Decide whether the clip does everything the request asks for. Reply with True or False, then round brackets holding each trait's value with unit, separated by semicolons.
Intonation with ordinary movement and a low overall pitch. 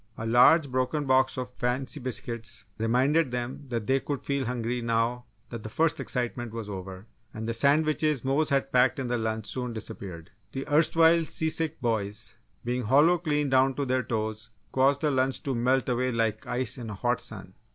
True (3.3 semitones; 125 Hz)